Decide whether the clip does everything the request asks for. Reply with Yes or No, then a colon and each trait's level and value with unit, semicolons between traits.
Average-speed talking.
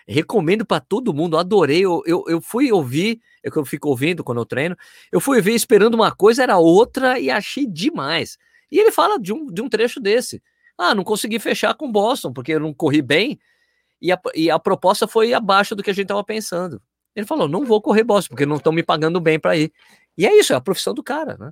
No: fast, 230 wpm